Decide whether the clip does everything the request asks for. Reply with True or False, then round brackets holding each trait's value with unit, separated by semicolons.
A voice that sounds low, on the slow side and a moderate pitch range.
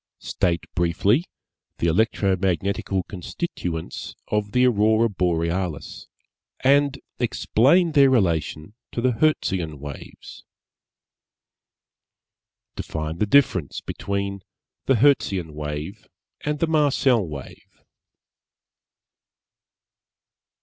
False (100 Hz; 85 wpm; 7.1 semitones)